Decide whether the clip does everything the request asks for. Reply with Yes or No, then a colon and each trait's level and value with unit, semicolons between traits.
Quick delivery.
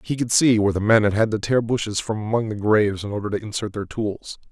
Yes: fast, 280 wpm